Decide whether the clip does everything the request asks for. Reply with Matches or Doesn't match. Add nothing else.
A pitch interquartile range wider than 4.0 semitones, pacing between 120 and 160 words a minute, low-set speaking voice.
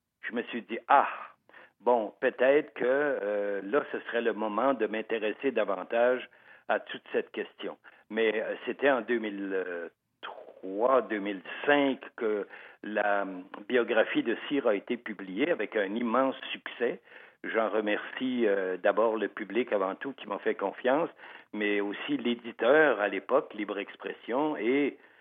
Matches